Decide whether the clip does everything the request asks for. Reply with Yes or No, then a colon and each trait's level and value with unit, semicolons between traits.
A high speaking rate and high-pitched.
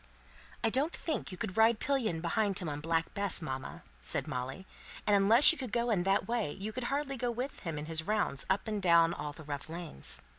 Yes: fast, 215 wpm; high, 195 Hz